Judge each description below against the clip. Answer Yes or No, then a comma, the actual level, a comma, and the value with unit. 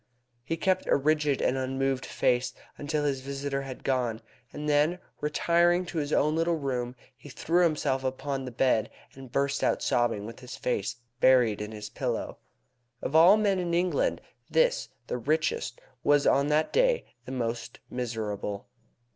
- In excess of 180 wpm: No, average, 165 wpm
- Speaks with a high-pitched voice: No, medium, 140 Hz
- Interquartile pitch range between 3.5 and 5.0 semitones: Yes, average, 4.2 semitones